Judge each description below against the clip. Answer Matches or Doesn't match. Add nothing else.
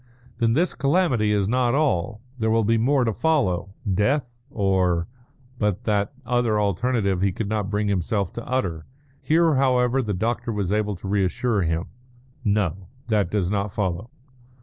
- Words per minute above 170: Doesn't match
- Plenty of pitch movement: Doesn't match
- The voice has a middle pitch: Doesn't match